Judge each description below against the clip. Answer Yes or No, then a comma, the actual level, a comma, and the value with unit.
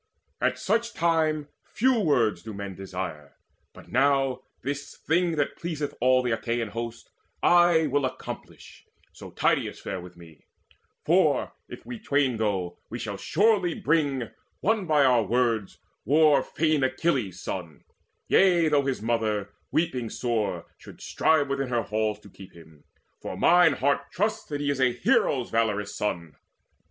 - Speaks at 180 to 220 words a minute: No, average, 150 wpm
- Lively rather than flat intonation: Yes, wide, 6.5 semitones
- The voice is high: No, low, 130 Hz